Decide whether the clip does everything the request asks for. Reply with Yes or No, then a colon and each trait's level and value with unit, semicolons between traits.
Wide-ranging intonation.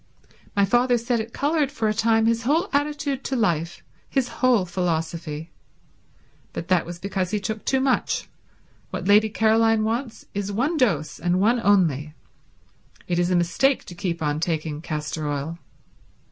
Yes: wide, 5.9 semitones